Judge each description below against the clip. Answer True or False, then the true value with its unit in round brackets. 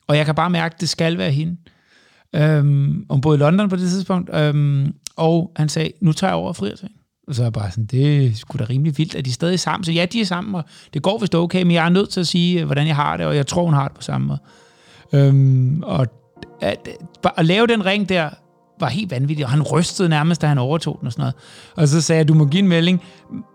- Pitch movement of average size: True (3.7 semitones)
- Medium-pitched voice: True (160 Hz)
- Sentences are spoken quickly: True (275 wpm)